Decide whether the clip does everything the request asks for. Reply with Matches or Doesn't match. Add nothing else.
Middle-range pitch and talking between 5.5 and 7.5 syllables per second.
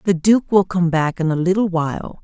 Doesn't match